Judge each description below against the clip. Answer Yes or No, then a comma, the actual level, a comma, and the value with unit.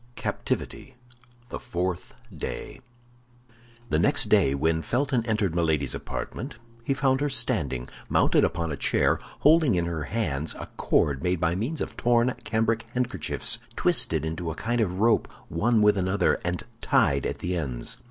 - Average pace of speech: Yes, average, 155 wpm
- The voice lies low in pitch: Yes, very low, 90 Hz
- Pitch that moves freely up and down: Yes, wide, 6.5 semitones